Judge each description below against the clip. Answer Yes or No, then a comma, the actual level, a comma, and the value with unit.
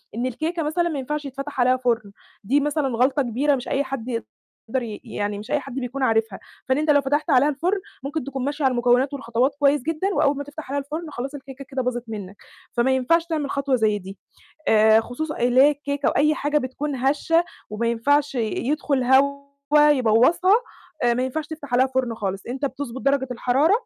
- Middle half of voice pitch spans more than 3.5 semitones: No, average, 3.1 semitones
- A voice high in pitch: Yes, very high, 270 Hz